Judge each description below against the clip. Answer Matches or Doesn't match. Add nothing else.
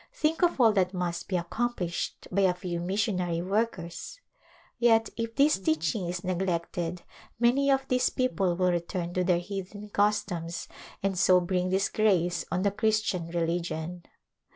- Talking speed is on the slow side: Doesn't match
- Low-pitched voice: Doesn't match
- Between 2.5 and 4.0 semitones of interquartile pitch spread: Matches